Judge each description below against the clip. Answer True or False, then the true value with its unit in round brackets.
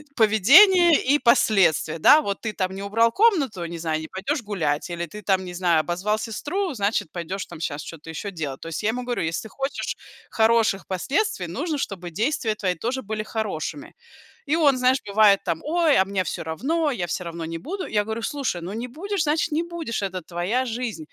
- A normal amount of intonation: False (7.6 semitones)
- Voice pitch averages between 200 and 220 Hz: True (215 Hz)